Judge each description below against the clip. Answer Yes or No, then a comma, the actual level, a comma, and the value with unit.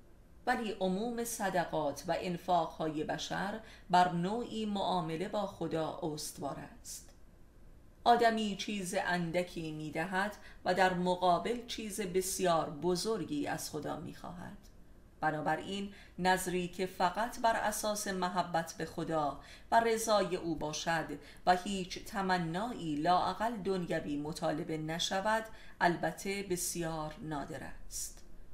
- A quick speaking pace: No, average, 110 wpm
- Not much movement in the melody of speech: No, average, 3.8 semitones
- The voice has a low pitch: No, medium, 180 Hz